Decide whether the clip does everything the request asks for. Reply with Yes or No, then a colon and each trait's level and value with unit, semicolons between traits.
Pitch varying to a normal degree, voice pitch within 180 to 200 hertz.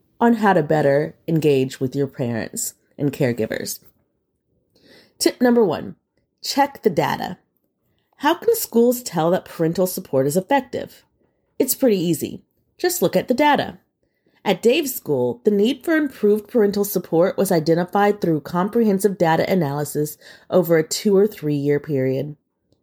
No: wide, 7.8 semitones; medium, 185 Hz